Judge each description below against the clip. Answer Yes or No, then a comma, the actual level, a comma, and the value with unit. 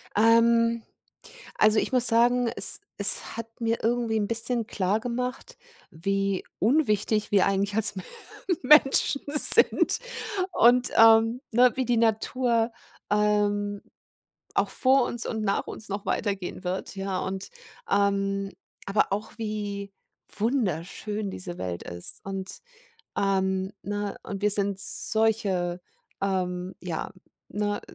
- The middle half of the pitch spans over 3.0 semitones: No, average, 2.7 semitones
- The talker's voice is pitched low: No, high, 210 Hz